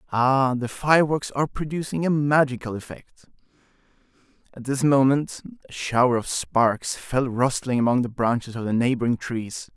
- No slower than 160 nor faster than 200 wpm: No, average, 150 wpm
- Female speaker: No, male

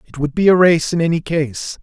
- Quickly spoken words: Yes, fast, 265 wpm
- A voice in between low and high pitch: Yes, medium, 160 Hz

